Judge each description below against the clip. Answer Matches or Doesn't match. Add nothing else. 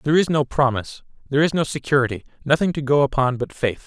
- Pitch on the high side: Doesn't match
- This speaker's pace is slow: Doesn't match